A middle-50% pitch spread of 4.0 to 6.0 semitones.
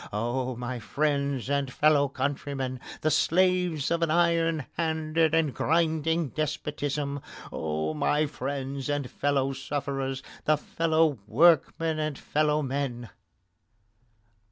No: average, 2.9 semitones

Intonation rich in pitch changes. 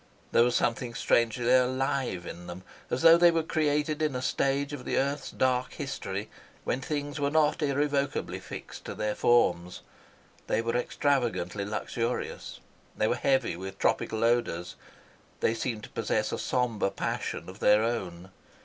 No: average, 4.8 semitones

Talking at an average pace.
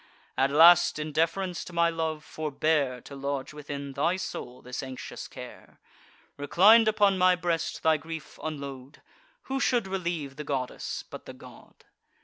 Yes: average, 150 wpm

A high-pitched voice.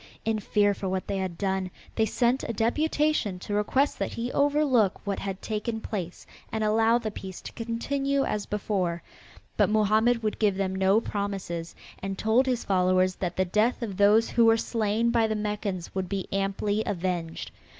Yes: high, 210 Hz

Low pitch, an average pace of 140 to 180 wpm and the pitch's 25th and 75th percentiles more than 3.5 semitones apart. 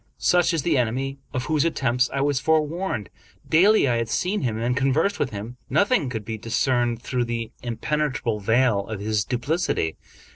Yes: low, 125 Hz; average, 175 wpm; average, 4.8 semitones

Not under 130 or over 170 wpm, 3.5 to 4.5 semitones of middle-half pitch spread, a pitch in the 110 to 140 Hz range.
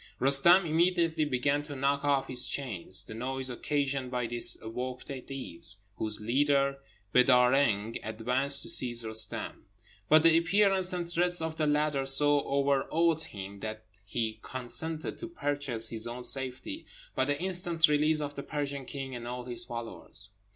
Yes: average, 160 wpm; average, 3.9 semitones; low, 135 Hz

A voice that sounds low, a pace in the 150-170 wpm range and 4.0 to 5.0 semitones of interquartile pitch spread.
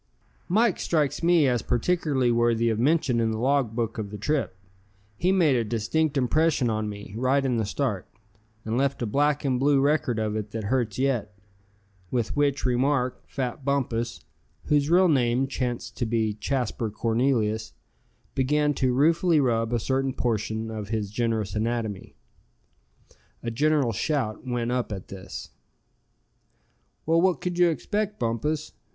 Yes: low, 125 Hz; average, 155 wpm; average, 4.4 semitones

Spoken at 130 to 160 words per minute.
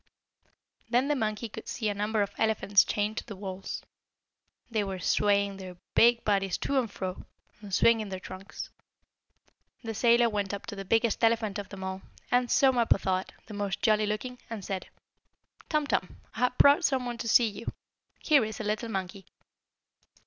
No: average, 185 wpm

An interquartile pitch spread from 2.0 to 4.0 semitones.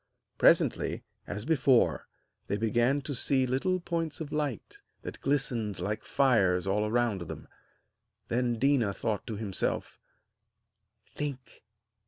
No: average, 4.9 semitones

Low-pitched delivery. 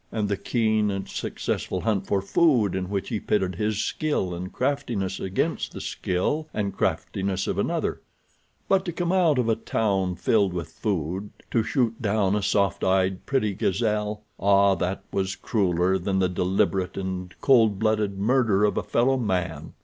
Yes: low, 100 Hz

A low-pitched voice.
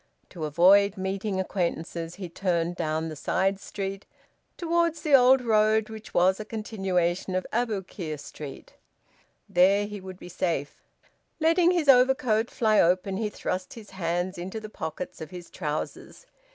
No: high, 195 Hz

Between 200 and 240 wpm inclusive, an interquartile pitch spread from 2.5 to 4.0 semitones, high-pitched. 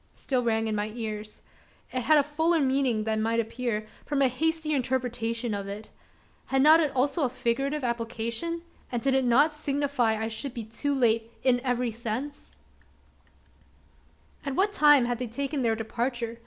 No: average, 170 wpm; average, 3.7 semitones; very high, 250 Hz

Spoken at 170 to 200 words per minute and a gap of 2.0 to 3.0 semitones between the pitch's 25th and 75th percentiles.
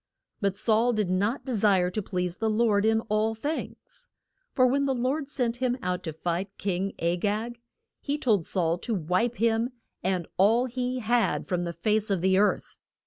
No: average, 190 wpm; average, 4.6 semitones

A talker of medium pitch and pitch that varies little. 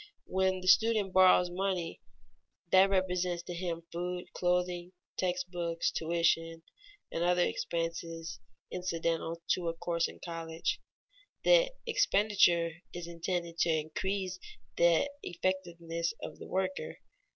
Yes: medium, 175 Hz; narrow, 1.8 semitones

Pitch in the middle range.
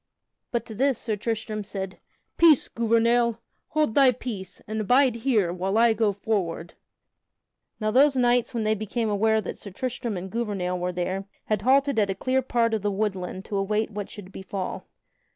No: high, 215 Hz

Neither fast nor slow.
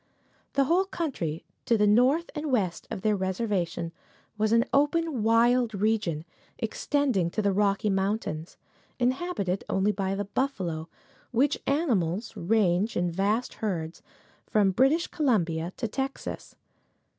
No: slow, 130 wpm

